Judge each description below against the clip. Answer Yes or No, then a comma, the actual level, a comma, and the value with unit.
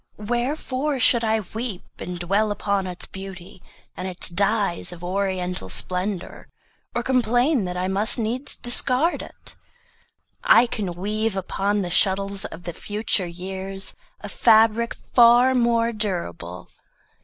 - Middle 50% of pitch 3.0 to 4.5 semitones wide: Yes, average, 4.2 semitones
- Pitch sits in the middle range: No, high, 200 Hz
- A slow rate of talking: Yes, slow, 130 wpm